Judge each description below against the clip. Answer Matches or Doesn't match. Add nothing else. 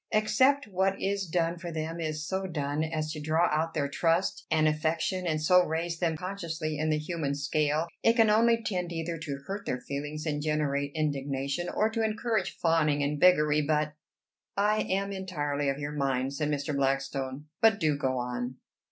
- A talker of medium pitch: Matches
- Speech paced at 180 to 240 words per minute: Matches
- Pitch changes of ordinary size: Matches